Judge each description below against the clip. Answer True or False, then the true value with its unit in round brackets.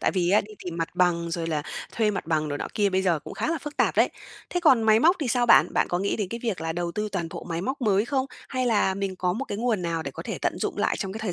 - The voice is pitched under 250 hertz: True (195 Hz)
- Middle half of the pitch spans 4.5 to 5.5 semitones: True (5.1 semitones)